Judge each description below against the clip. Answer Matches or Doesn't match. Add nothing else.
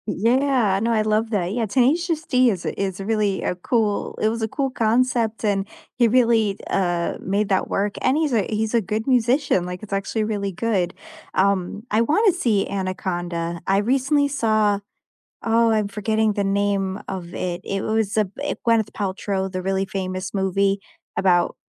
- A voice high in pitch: Matches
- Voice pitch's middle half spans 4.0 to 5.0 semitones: Doesn't match